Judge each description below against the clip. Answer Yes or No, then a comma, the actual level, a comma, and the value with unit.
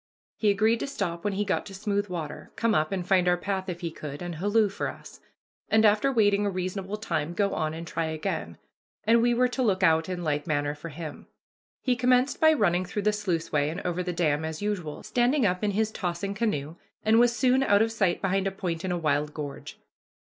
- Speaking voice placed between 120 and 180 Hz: No, high, 190 Hz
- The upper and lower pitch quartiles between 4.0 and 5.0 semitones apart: Yes, average, 4.3 semitones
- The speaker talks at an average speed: No, fast, 230 wpm